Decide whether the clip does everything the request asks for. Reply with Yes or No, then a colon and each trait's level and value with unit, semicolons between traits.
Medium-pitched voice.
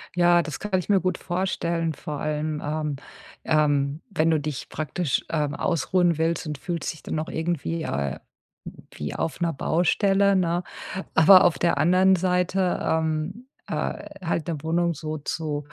Yes: medium, 165 Hz